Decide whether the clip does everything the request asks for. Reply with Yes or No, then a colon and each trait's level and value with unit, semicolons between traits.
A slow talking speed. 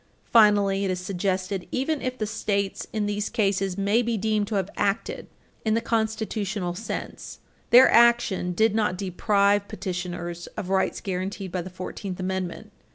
No: average, 160 wpm